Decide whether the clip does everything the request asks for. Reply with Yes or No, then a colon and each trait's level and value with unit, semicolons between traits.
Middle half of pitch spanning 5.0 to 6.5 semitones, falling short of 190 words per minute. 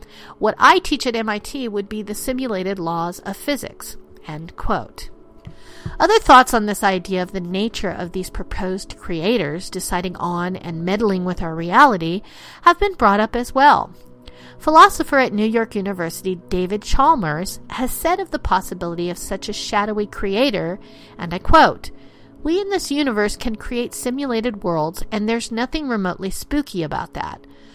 Yes: wide, 5.5 semitones; average, 160 wpm